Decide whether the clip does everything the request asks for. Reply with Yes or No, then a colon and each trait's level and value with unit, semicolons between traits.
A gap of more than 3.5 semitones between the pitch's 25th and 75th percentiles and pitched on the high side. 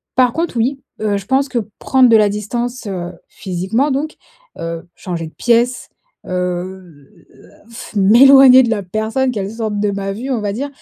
Yes: average, 4.9 semitones; high, 220 Hz